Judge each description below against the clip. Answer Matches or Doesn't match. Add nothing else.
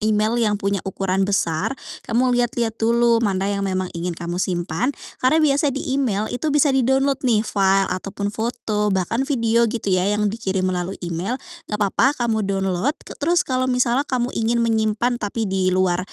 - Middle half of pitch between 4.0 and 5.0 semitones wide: Matches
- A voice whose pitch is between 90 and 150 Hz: Doesn't match